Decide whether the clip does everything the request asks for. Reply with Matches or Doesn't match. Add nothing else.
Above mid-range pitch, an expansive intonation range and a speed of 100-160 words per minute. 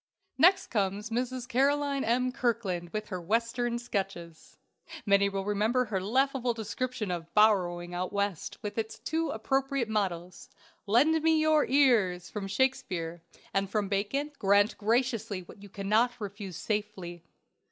Doesn't match